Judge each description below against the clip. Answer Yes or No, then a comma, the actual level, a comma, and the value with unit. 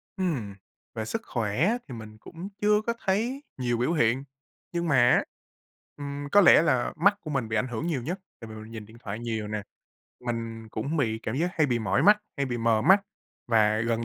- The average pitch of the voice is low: Yes, low, 125 Hz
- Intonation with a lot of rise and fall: Yes, wide, 7.2 semitones